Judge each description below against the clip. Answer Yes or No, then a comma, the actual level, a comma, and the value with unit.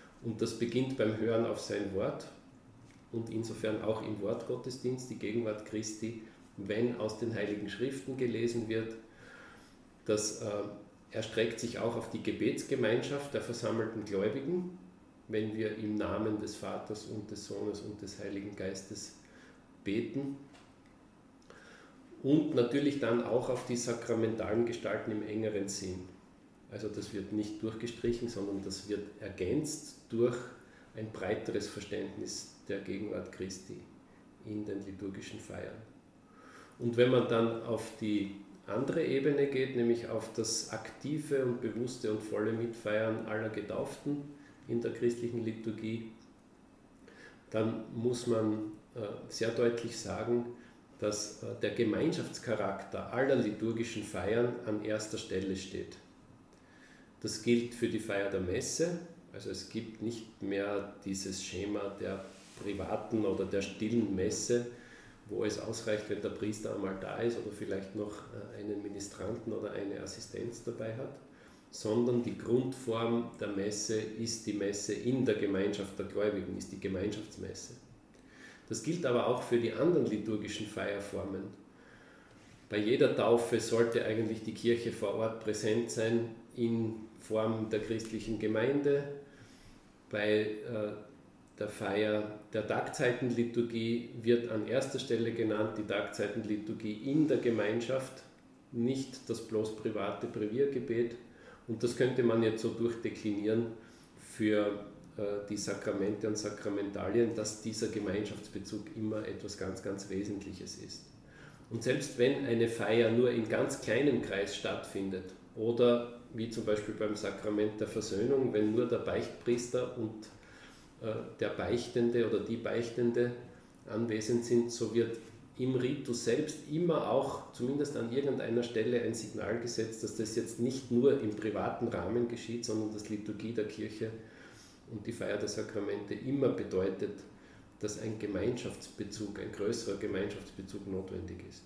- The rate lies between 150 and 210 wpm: No, average, 135 wpm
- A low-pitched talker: Yes, low, 110 Hz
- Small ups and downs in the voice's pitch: Yes, narrow, 2.2 semitones